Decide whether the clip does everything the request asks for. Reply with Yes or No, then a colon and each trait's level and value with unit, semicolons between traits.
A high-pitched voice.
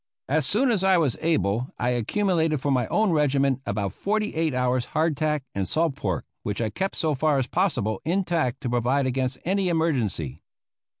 No: medium, 140 Hz